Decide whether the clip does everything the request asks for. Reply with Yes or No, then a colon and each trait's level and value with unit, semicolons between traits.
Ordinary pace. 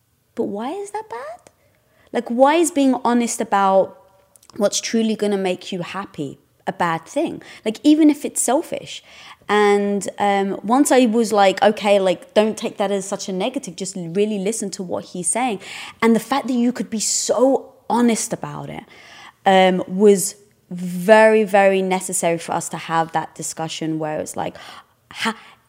Yes: average, 175 wpm